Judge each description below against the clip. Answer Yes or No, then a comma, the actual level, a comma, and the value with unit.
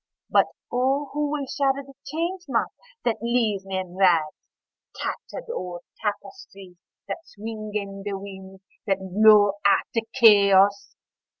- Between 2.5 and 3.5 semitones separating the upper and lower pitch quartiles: No, average, 4.9 semitones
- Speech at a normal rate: No, slow, 130 wpm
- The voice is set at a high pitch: Yes, high, 205 Hz